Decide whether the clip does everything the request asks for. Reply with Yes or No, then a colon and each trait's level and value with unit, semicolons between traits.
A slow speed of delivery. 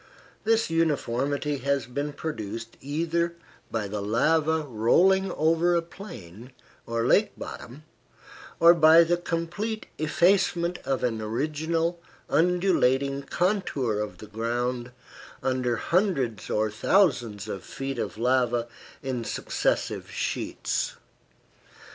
Yes: slow, 110 wpm